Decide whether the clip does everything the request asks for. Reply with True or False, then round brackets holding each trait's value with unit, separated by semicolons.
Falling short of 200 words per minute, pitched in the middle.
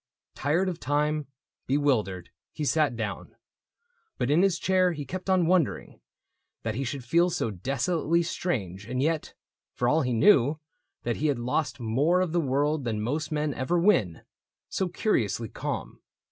True (170 wpm; 145 Hz)